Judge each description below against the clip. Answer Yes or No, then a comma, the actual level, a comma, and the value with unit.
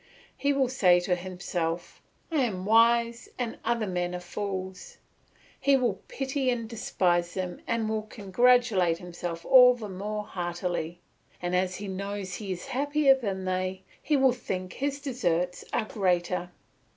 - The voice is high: Yes, high, 195 Hz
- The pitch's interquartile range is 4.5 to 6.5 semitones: Yes, average, 5.1 semitones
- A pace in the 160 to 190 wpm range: No, average, 150 wpm